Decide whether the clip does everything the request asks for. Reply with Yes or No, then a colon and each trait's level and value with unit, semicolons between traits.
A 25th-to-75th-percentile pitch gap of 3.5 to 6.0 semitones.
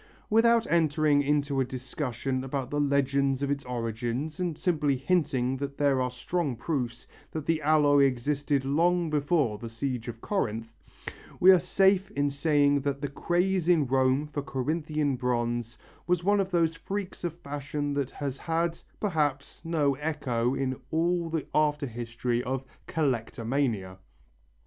Yes: average, 3.8 semitones